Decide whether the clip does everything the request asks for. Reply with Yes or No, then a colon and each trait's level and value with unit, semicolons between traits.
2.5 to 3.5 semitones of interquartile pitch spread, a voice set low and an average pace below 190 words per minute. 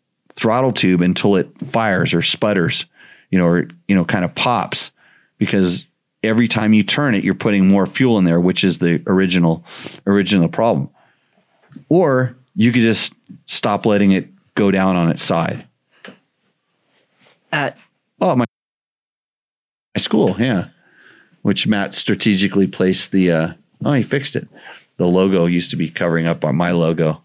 Yes: average, 2.8 semitones; very low, 95 Hz; average, 155 wpm